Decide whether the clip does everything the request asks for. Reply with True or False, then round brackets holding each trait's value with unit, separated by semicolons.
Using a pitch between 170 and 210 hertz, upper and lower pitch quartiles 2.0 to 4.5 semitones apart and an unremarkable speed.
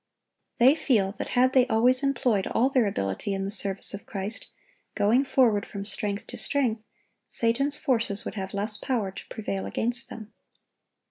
False (220 Hz; 4.0 semitones; 165 wpm)